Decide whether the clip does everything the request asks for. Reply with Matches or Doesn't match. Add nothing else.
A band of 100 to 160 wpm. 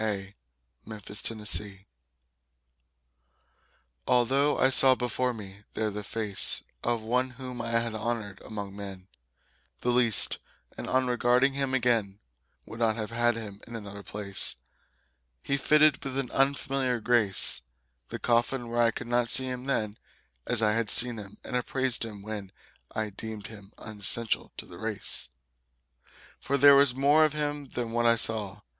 Matches